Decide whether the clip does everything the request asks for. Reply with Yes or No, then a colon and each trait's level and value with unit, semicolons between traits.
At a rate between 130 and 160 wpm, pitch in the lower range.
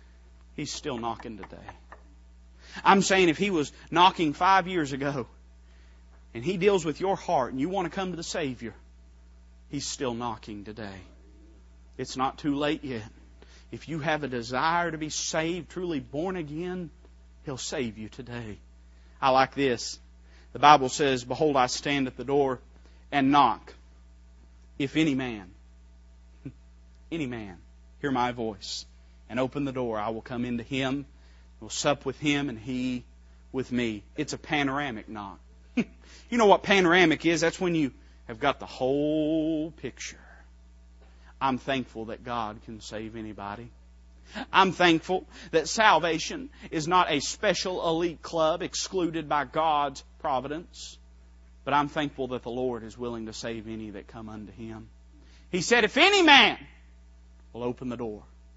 Yes: average, 155 wpm; low, 120 Hz